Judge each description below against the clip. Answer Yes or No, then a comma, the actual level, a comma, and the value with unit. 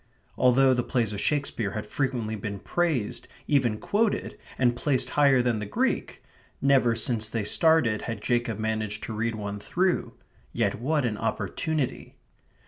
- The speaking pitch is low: Yes, low, 120 Hz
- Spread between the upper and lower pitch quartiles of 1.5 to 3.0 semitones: No, average, 4.3 semitones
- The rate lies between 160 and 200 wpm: No, average, 150 wpm